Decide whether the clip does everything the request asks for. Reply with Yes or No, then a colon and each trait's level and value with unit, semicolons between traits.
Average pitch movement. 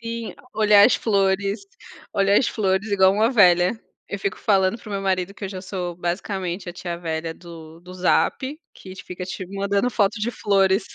No: narrow, 2.2 semitones